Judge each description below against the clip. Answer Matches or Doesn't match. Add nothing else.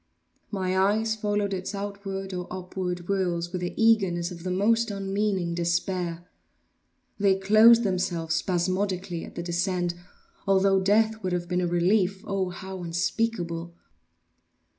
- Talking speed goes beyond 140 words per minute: Doesn't match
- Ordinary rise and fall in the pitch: Doesn't match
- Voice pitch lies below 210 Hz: Matches